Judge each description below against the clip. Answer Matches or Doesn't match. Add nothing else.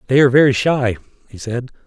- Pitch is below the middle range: Matches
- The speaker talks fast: Doesn't match